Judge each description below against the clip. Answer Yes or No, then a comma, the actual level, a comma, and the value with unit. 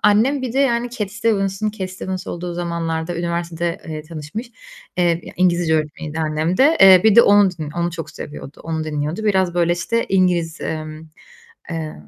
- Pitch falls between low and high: Yes, medium, 175 Hz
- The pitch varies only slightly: No, average, 3.9 semitones